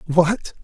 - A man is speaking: Yes, male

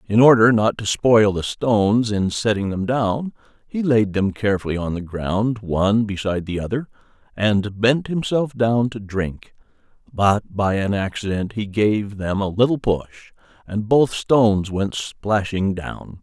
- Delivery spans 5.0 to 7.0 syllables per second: No, 4.2 syllables/s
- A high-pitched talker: No, low, 105 Hz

